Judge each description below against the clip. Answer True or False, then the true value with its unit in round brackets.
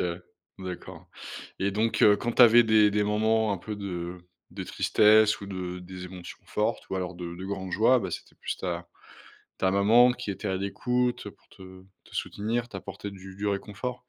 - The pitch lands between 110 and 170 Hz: False (100 Hz)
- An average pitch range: True (3.0 semitones)